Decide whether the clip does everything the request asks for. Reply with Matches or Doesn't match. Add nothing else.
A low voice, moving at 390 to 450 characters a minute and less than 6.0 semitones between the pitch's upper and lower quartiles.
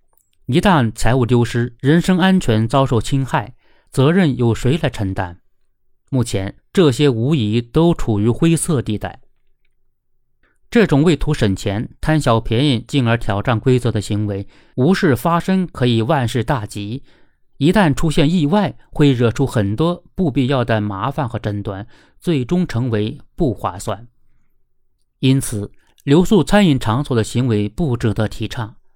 Doesn't match